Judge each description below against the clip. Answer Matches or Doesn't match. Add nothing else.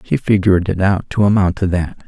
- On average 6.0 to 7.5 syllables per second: Doesn't match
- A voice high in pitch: Doesn't match